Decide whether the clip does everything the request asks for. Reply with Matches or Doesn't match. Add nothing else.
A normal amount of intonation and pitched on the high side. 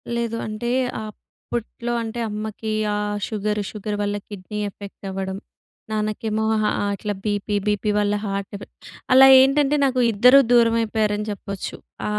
Doesn't match